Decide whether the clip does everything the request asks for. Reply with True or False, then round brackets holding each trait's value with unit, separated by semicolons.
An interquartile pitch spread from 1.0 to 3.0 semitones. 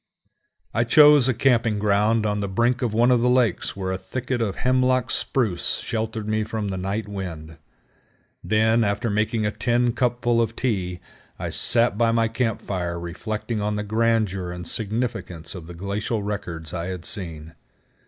False (3.6 semitones)